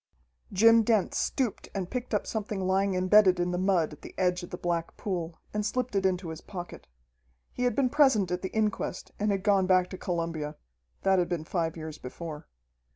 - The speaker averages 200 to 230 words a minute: Yes, fast, 205 wpm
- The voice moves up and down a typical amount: Yes, average, 3.3 semitones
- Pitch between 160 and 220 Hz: Yes, medium, 185 Hz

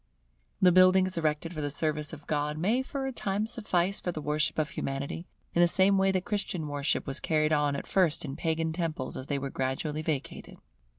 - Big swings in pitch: No, average, 3.8 semitones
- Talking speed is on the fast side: Yes, fast, 210 wpm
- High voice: No, medium, 160 Hz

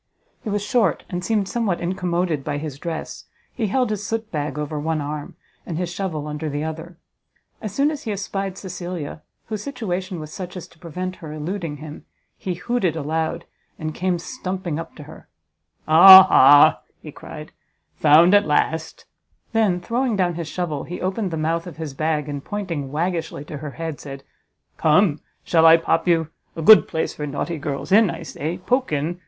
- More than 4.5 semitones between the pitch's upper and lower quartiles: No, average, 3.7 semitones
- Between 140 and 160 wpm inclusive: No, average, 185 wpm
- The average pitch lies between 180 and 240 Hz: No, medium, 170 Hz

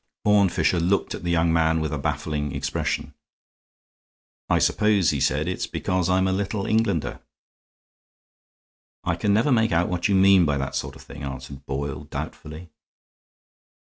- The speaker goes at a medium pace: Yes, average, 160 wpm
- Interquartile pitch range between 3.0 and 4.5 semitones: No, average, 4.9 semitones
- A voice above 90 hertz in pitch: No, very low, 85 Hz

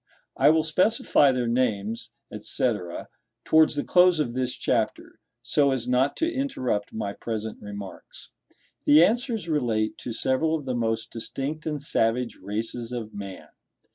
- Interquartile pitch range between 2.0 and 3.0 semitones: No, wide, 5.4 semitones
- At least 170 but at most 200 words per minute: No, average, 145 wpm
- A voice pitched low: Yes, low, 125 Hz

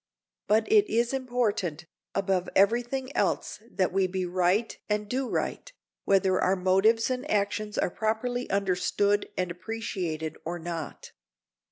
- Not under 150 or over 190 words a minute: No, average, 140 wpm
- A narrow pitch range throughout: No, average, 4.2 semitones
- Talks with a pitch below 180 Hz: No, high, 200 Hz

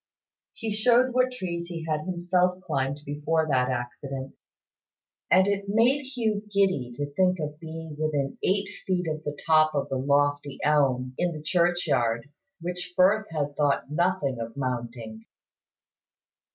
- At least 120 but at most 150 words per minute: Yes, average, 145 wpm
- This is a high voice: No, medium, 155 Hz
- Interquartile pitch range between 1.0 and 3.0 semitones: No, average, 4.7 semitones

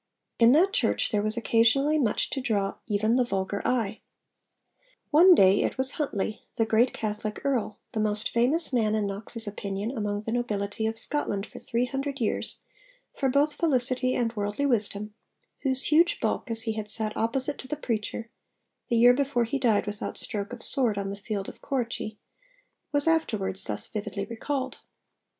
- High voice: Yes, high, 230 Hz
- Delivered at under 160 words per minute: No, average, 175 wpm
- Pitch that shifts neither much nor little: Yes, average, 4.0 semitones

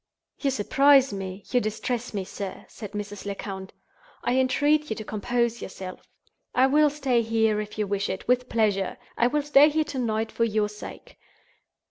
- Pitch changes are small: No, average, 4.2 semitones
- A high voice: Yes, high, 225 Hz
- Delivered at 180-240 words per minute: No, average, 165 wpm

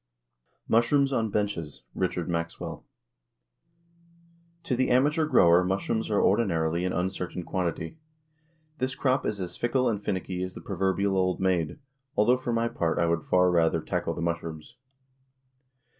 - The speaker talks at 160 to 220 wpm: No, average, 145 wpm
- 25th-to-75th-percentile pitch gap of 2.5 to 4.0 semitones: No, wide, 5.4 semitones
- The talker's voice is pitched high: No, very low, 95 Hz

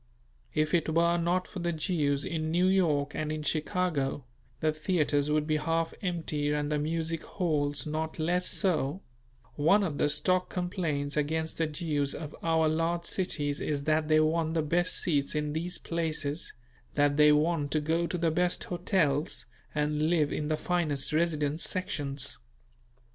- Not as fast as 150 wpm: No, average, 165 wpm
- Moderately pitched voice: Yes, medium, 155 Hz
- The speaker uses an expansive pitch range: No, narrow, 2.4 semitones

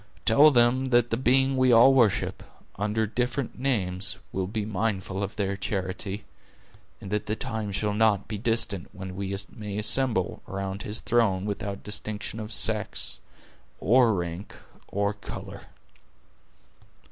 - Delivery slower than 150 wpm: Yes, average, 140 wpm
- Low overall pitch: Yes, low, 105 Hz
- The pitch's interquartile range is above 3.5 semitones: No, average, 3.1 semitones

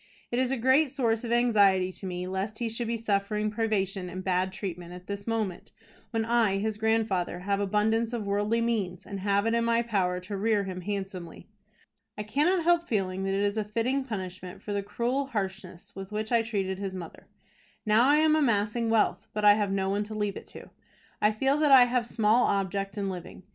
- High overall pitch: Yes, high, 210 Hz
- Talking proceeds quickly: Yes, fast, 210 wpm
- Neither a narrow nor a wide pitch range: Yes, average, 3.1 semitones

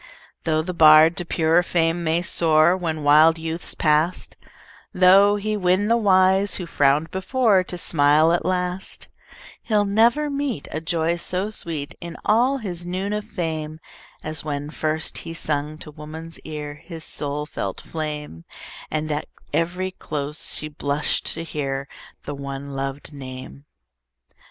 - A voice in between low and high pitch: Yes, medium, 165 Hz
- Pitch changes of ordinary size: Yes, average, 3.5 semitones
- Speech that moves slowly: No, average, 150 wpm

